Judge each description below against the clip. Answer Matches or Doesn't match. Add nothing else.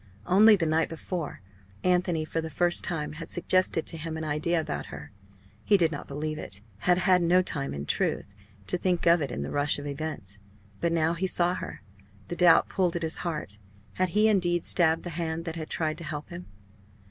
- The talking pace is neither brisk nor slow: Doesn't match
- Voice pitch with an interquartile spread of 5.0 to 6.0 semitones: Doesn't match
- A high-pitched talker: Doesn't match